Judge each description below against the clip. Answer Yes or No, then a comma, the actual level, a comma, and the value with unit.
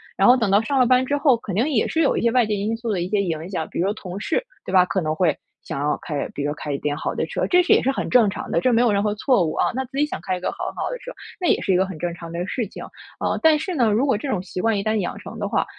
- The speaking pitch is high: Yes, high, 210 Hz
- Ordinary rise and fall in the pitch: No, wide, 6.0 semitones